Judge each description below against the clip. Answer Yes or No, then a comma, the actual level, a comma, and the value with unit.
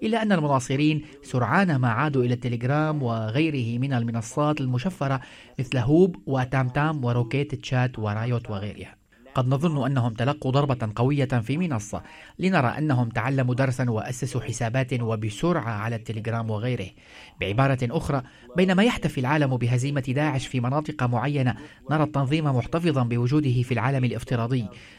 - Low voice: Yes, low, 130 Hz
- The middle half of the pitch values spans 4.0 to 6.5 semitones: No, average, 3.3 semitones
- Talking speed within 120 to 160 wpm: Yes, average, 130 wpm